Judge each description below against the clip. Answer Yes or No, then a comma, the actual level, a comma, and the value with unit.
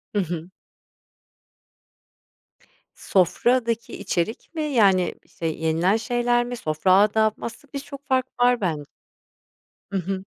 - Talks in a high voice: Yes, high, 215 Hz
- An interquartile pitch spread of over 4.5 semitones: Yes, average, 5.3 semitones